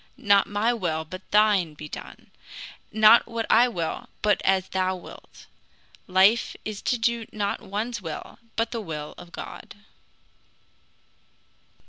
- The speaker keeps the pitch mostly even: No, average, 3.4 semitones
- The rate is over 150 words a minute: No, slow, 135 wpm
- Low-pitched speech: No, high, 205 Hz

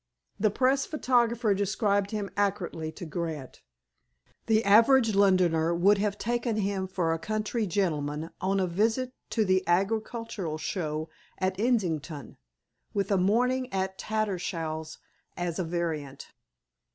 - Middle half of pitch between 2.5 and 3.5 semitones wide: No, average, 4.3 semitones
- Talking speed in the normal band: No, slow, 130 wpm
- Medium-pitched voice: No, high, 195 Hz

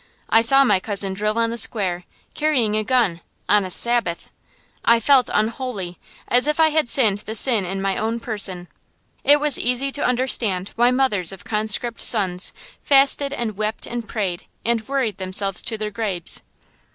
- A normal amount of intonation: Yes, average, 4.2 semitones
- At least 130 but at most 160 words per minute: No, average, 175 wpm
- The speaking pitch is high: Yes, high, 220 Hz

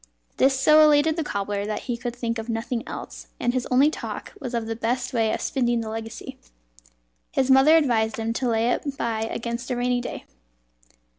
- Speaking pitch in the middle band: No, high, 240 Hz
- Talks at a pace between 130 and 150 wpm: No, average, 200 wpm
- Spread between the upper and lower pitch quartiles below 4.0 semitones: Yes, average, 2.8 semitones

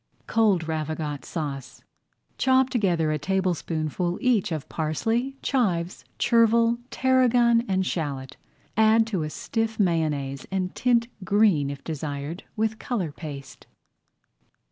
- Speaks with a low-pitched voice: No, medium, 185 Hz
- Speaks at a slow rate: Yes, slow, 115 wpm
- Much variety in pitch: Yes, wide, 6.7 semitones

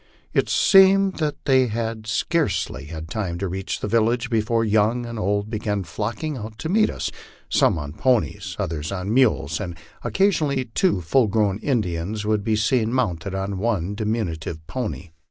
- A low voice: Yes, low, 110 Hz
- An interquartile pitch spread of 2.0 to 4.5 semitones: Yes, average, 4.2 semitones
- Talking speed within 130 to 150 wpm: No, average, 165 wpm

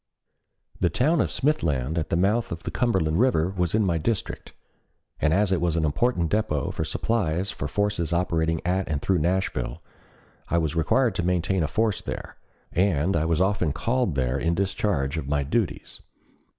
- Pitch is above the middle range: No, very low, 85 Hz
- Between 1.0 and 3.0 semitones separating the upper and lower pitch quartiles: No, average, 4.5 semitones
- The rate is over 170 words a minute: Yes, average, 185 wpm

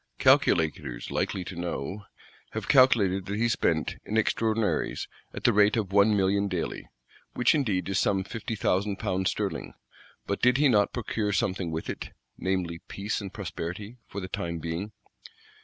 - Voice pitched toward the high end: No, low, 100 Hz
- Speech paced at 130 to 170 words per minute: Yes, average, 160 wpm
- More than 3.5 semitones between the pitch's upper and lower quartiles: No, average, 2.8 semitones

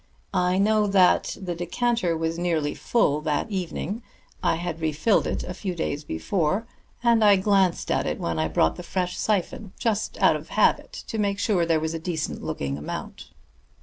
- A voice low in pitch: No, medium, 180 Hz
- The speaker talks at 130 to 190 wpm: Yes, average, 180 wpm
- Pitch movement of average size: Yes, average, 4.1 semitones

